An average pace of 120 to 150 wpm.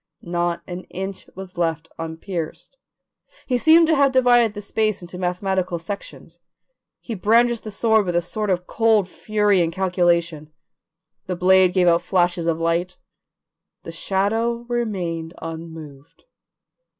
Yes: average, 140 wpm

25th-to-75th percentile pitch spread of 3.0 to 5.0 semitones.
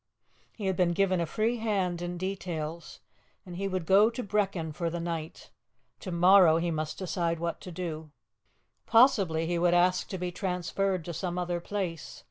No: narrow, 2.4 semitones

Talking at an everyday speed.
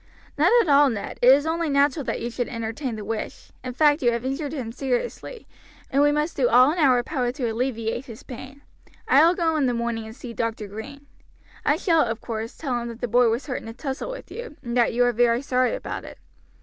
No: fast, 240 wpm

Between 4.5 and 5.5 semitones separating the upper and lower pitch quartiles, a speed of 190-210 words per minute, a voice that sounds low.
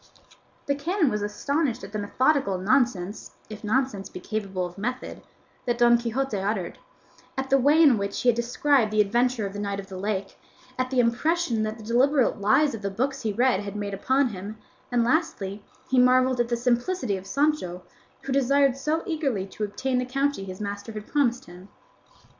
No: average, 4.8 semitones; average, 195 wpm; high, 235 Hz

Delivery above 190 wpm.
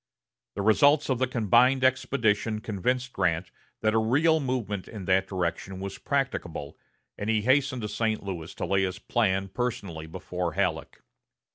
No: average, 155 wpm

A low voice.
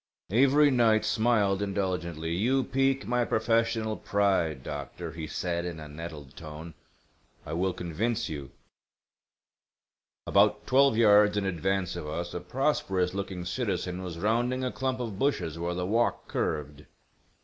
Yes: very low, 95 Hz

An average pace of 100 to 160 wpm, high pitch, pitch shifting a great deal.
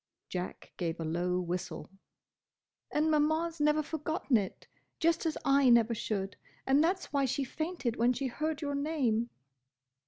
Yes: average, 155 wpm; very high, 275 Hz; wide, 6.0 semitones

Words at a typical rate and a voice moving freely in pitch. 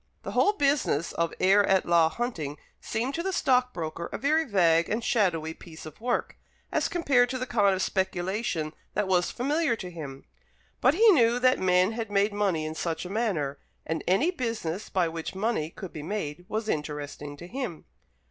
Yes: average, 185 wpm; wide, 6.7 semitones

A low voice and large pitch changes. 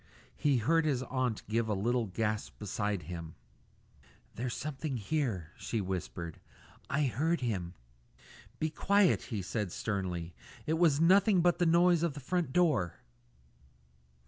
Yes: low, 125 Hz; wide, 8.2 semitones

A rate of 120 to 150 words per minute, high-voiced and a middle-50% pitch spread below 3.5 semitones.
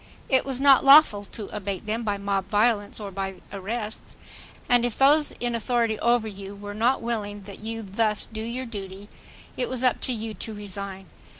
No: average, 190 wpm; high, 220 Hz; average, 3.0 semitones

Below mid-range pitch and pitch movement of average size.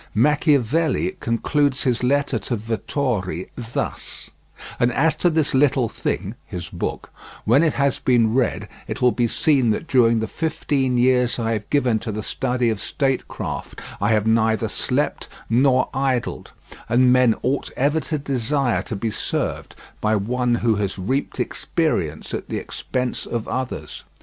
Yes: low, 125 Hz; average, 3.5 semitones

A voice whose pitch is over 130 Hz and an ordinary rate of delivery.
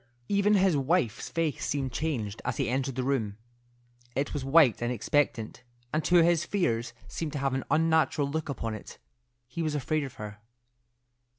Yes: medium, 140 Hz; average, 175 wpm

